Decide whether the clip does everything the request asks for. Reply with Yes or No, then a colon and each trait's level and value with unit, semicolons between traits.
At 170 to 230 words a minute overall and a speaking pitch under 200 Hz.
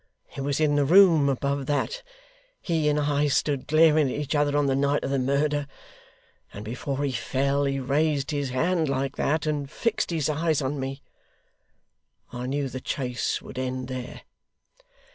Yes: average, 175 wpm; medium, 140 Hz